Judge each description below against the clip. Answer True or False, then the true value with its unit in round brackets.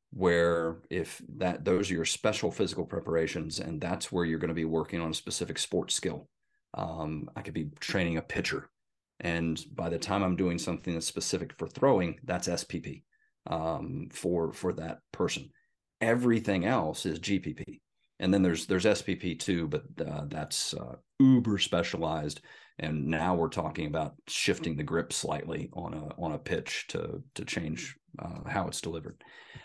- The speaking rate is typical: True (170 wpm)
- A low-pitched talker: True (85 Hz)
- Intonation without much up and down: False (3.1 semitones)